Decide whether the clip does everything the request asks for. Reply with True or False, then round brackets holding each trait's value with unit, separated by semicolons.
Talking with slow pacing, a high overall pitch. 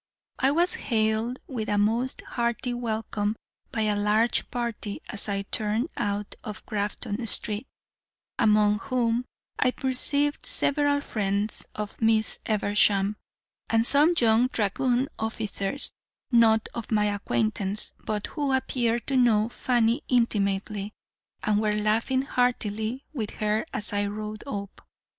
True (130 wpm; 220 Hz)